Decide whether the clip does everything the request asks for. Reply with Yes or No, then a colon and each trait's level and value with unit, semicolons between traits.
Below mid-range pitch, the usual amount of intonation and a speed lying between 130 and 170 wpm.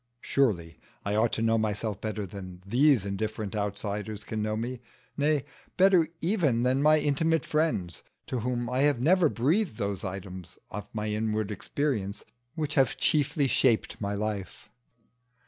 No: low, 110 Hz; wide, 5.8 semitones; average, 150 wpm